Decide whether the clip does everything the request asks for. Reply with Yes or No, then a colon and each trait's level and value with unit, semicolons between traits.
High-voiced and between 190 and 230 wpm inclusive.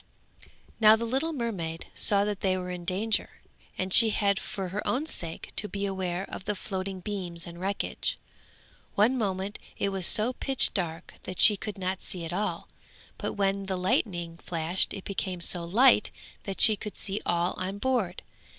No: high, 195 Hz; average, 180 wpm